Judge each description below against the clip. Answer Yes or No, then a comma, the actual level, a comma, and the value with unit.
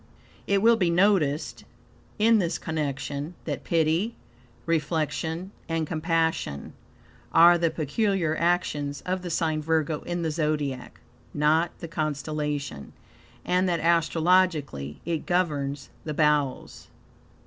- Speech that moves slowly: Yes, slow, 115 wpm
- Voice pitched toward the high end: No, medium, 160 Hz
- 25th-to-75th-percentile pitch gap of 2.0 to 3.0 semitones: Yes, average, 2.7 semitones